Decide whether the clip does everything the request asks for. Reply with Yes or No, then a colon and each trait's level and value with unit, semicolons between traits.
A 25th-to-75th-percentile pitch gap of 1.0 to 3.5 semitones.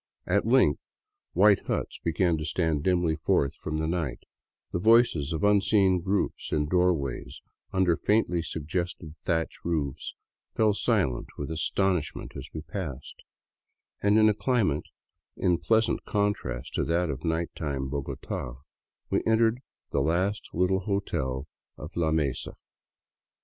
No: average, 4.6 semitones